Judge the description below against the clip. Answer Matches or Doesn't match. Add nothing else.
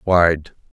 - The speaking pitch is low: Matches